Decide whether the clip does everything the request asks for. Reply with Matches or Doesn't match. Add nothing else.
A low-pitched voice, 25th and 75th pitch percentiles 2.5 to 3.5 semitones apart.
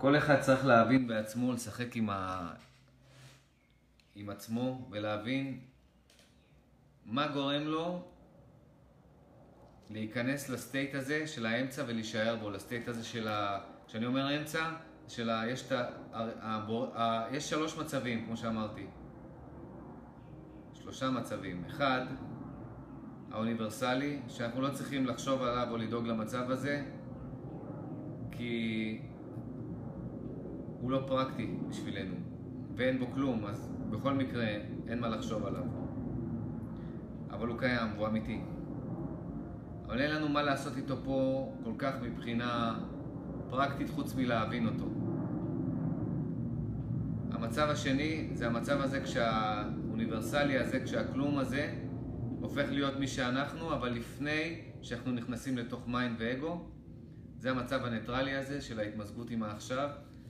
Matches